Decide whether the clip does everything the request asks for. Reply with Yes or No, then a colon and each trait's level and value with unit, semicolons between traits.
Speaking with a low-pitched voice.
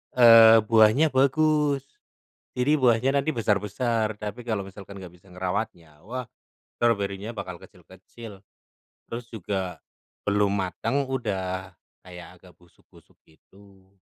Yes: low, 105 Hz